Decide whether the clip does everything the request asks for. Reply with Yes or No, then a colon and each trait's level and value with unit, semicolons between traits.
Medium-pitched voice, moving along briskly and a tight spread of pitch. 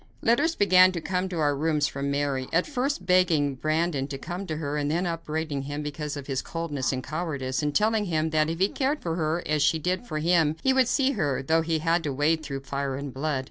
No: medium, 155 Hz; fast, 240 wpm; average, 3.8 semitones